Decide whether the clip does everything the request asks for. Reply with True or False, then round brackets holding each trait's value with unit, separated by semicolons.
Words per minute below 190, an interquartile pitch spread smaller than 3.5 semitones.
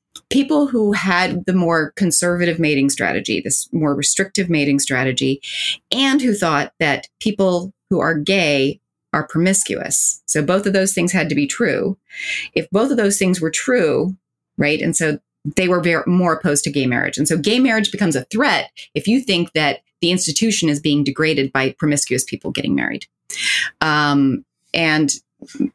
False (170 wpm; 4.8 semitones)